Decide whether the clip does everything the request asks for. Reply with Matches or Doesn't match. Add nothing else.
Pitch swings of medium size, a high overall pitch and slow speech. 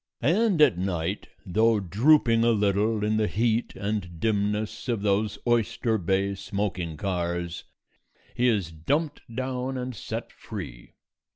Doesn't match